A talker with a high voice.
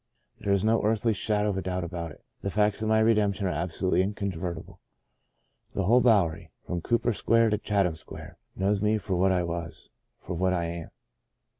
No: low, 100 Hz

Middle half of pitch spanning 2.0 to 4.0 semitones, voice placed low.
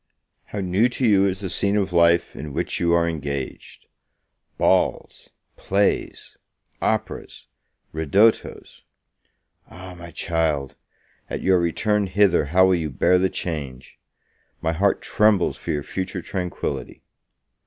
Yes: average, 3.4 semitones; very low, 90 Hz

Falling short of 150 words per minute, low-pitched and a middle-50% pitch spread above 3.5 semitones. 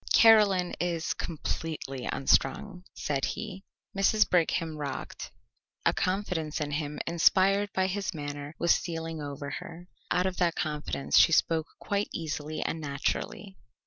No: slow, 135 wpm; medium, 165 Hz; average, 3.9 semitones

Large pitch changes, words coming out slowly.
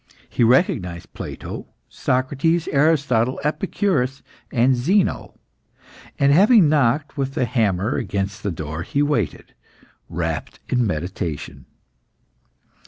Yes: wide, 6.6 semitones; slow, 100 wpm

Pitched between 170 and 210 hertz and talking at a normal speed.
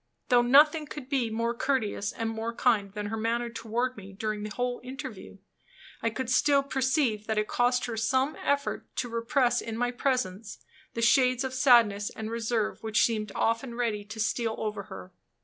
No: high, 235 Hz; average, 185 wpm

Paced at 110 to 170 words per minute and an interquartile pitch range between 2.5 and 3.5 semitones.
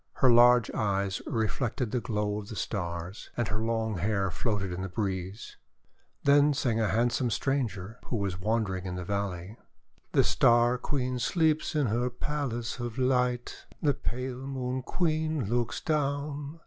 No: average, 160 wpm; average, 4.3 semitones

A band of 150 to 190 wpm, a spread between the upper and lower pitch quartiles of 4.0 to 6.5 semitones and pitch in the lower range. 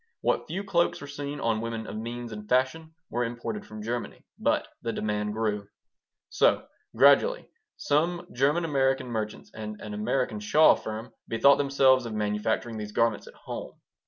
Yes: average, 160 wpm; average, 4.6 semitones; low, 115 Hz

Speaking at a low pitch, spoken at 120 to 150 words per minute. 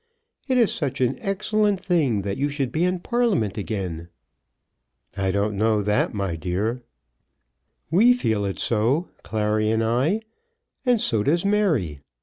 Yes: low, 120 Hz; average, 145 wpm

